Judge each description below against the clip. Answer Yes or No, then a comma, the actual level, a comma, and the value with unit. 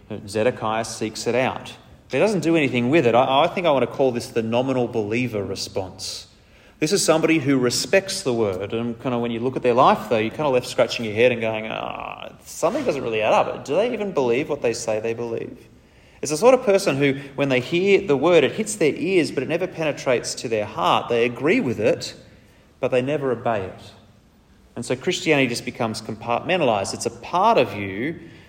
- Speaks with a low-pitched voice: Yes, low, 125 Hz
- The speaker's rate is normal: No, fast, 225 wpm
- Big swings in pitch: Yes, wide, 5.9 semitones